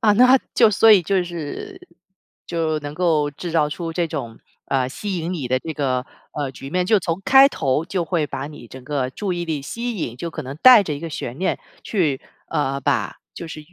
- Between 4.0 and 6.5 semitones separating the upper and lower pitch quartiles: Yes, average, 4.7 semitones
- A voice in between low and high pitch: Yes, medium, 165 Hz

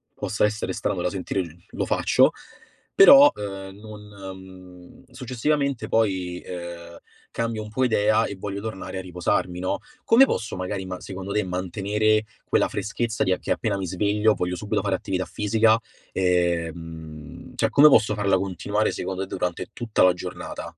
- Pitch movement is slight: No, average, 3.1 semitones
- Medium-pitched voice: No, very low, 95 Hz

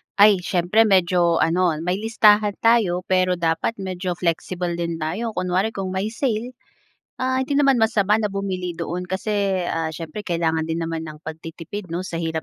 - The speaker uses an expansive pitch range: No, average, 3.7 semitones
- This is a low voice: No, medium, 185 Hz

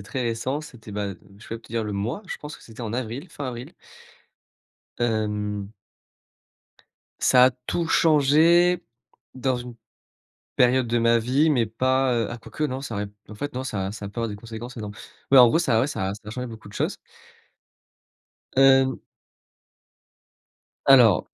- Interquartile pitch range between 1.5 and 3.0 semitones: No, average, 3.4 semitones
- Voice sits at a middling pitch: No, low, 120 Hz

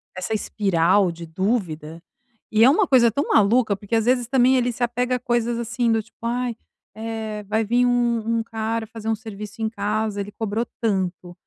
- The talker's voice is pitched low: No, high, 225 Hz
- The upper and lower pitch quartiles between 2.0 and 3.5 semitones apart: Yes, average, 2.7 semitones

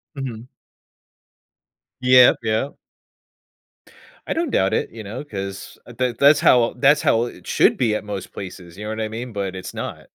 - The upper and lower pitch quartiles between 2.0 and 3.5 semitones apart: No, average, 4.0 semitones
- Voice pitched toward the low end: Yes, low, 115 Hz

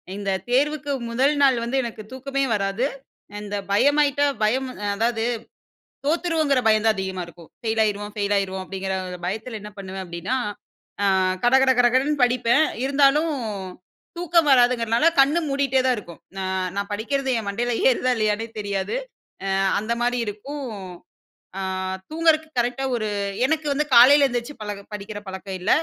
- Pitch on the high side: Yes, high, 240 Hz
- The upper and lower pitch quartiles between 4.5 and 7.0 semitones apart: Yes, average, 5.0 semitones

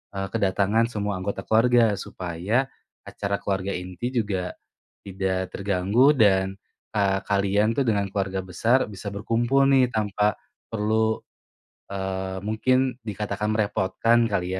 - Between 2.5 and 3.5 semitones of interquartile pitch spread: Yes, average, 2.9 semitones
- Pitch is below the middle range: Yes, low, 100 Hz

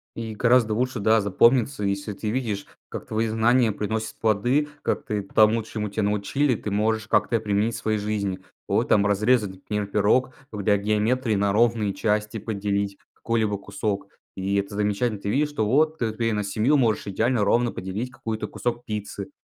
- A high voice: No, low, 110 Hz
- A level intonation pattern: Yes, narrow, 2.3 semitones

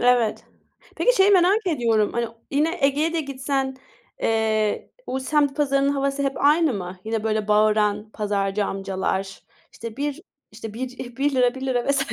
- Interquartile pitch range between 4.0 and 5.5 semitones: Yes, average, 4.7 semitones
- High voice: Yes, very high, 255 Hz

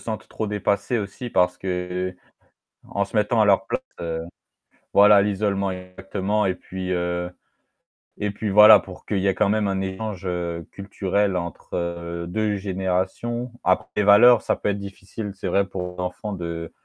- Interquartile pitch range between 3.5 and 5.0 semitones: No, narrow, 2.4 semitones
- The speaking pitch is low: Yes, very low, 95 Hz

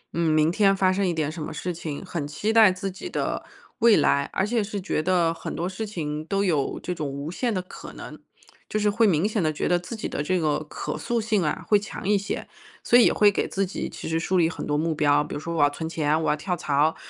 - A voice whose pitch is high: No, medium, 175 Hz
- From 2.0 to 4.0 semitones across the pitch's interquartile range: No, average, 4.5 semitones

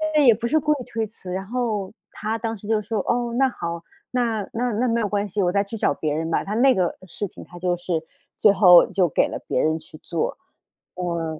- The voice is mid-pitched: No, high, 205 Hz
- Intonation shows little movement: No, average, 4.8 semitones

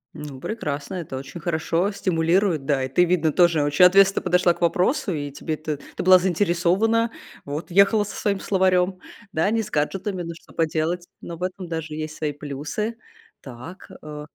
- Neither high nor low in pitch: Yes, medium, 170 Hz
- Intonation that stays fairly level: No, average, 3.7 semitones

